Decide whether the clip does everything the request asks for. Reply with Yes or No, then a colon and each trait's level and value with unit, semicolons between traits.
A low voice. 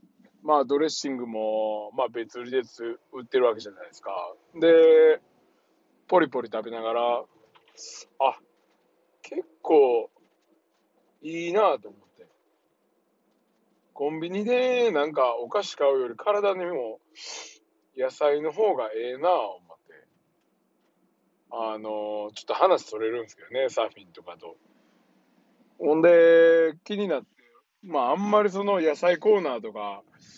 No: medium, 160 Hz